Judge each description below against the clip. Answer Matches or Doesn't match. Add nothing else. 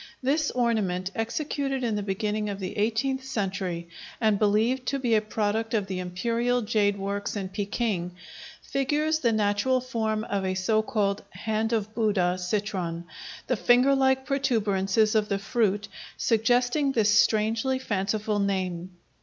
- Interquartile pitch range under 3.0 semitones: Doesn't match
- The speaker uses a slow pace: Doesn't match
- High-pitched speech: Matches